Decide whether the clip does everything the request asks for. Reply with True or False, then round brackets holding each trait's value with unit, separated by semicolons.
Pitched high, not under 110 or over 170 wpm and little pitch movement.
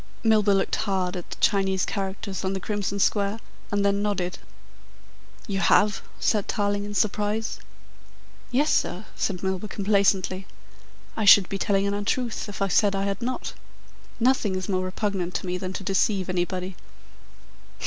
True (200 Hz; 160 wpm; 1.5 semitones)